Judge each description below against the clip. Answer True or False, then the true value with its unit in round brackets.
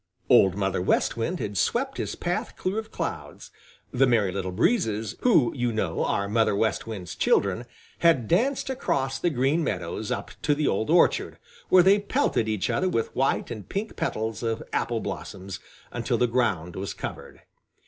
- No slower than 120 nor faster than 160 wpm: False (175 wpm)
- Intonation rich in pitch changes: True (9.0 semitones)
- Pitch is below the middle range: True (115 Hz)